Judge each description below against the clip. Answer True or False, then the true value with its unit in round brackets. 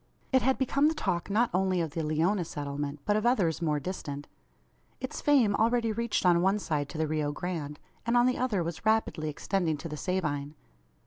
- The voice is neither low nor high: True (180 Hz)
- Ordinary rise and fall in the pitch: False (6.4 semitones)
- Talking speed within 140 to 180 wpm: False (200 wpm)